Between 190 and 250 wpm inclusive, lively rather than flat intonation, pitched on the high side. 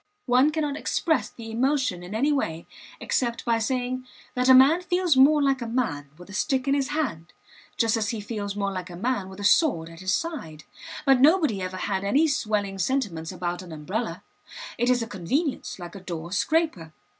Yes: average, 200 wpm; wide, 6.6 semitones; high, 230 Hz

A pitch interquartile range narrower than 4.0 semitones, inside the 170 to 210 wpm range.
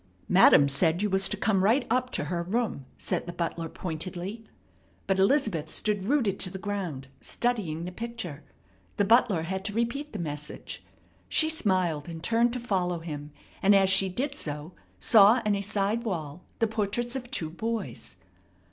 No: average, 5.2 semitones; average, 175 wpm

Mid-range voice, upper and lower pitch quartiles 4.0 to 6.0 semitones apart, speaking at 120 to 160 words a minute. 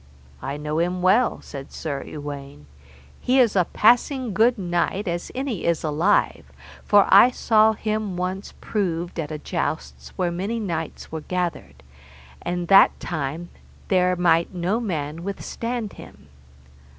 Yes: medium, 180 Hz; average, 4.8 semitones; average, 140 wpm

